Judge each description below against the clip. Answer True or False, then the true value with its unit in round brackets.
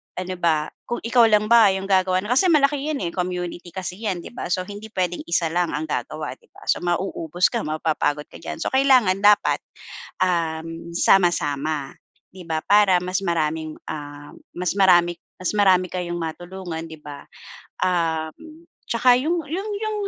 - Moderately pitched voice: True (180 Hz)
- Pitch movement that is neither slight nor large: True (4.0 semitones)